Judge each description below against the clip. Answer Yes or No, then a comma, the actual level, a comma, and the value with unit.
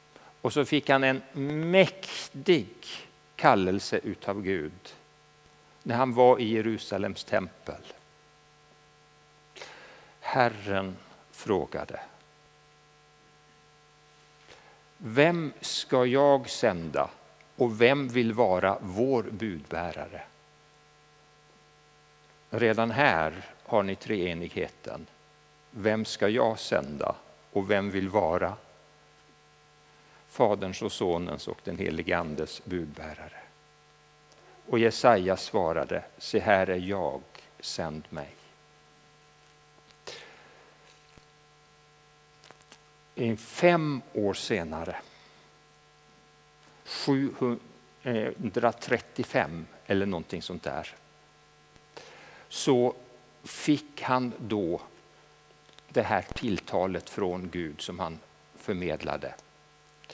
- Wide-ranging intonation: Yes, wide, 6.0 semitones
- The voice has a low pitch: Yes, very low, 75 Hz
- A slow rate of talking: Yes, slow, 80 wpm